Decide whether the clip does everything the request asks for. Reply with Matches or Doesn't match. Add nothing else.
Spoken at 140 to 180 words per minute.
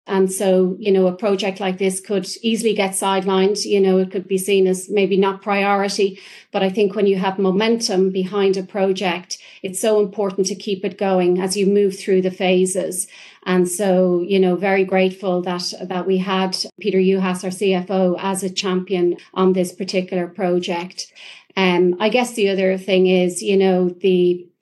Doesn't match